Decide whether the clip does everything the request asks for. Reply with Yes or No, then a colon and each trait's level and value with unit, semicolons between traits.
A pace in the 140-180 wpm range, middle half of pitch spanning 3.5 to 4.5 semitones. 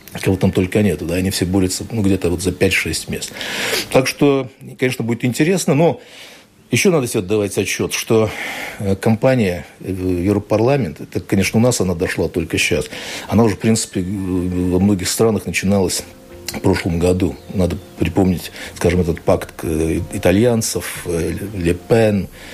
Yes: average, 145 wpm; average, 4.0 semitones